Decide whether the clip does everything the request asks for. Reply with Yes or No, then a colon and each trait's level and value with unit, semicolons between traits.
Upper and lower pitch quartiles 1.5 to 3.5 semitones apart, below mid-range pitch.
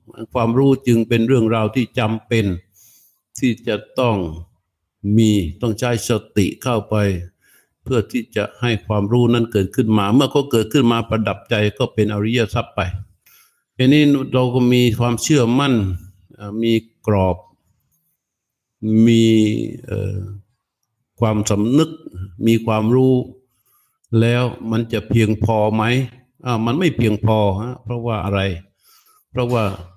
Yes: average, 2.8 semitones; low, 115 Hz